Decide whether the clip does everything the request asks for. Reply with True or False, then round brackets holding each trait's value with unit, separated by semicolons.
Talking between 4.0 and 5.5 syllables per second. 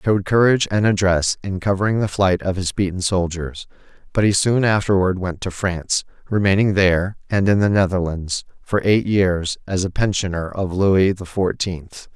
True (5.1 syllables/s)